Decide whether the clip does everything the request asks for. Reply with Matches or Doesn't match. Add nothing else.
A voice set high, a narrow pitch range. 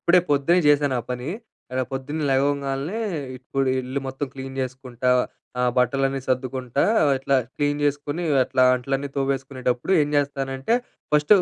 Doesn't match